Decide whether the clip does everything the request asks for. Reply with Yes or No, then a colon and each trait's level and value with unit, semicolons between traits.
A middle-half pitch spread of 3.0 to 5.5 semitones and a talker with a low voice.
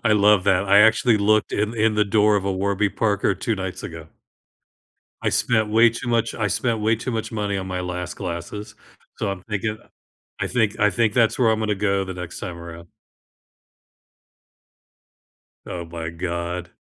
Yes: average, 3.3 semitones; low, 100 Hz